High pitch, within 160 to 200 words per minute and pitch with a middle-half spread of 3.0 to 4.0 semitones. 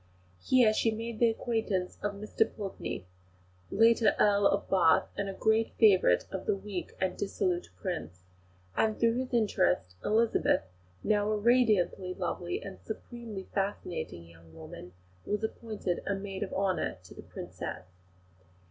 No: high, 200 Hz; average, 140 wpm; average, 3.3 semitones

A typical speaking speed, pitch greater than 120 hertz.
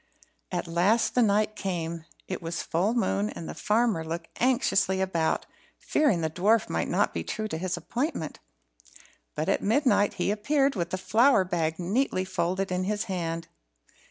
Yes: average, 165 wpm; medium, 185 Hz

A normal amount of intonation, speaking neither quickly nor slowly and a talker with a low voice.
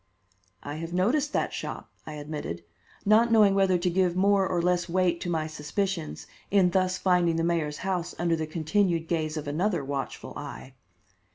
No: average, 3.3 semitones; average, 175 wpm; medium, 175 Hz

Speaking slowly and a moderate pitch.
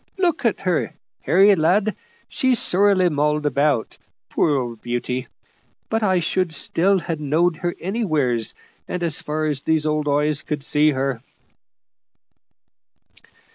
Yes: slow, 130 wpm; medium, 155 Hz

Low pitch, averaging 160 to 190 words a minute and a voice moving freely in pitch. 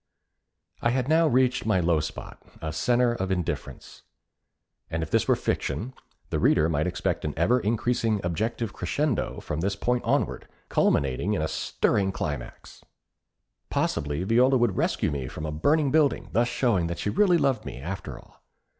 Yes: low, 100 Hz; average, 165 wpm; wide, 7.2 semitones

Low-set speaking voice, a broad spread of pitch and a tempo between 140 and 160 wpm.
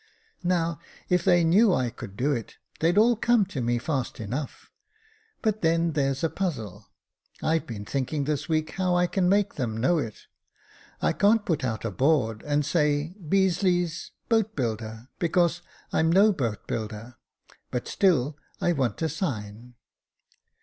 No: medium, 155 Hz; wide, 6.6 semitones; average, 155 wpm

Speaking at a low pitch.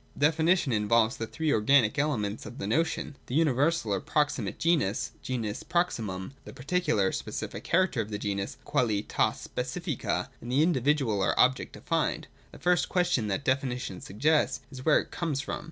Yes: low, 130 Hz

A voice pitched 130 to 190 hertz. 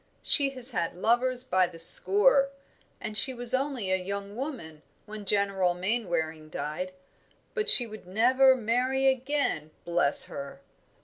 No: high, 215 Hz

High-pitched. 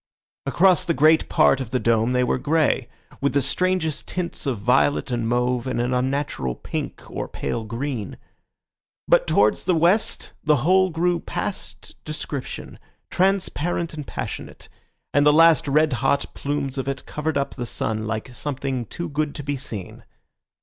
No: medium, 140 Hz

